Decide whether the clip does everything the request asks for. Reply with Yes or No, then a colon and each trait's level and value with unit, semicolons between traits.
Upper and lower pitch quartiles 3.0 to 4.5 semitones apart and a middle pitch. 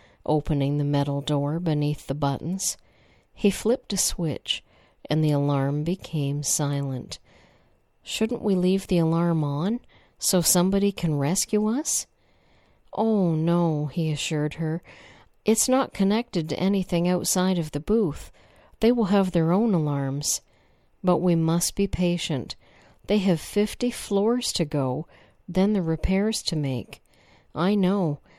No: average, 5.0 semitones; medium, 170 Hz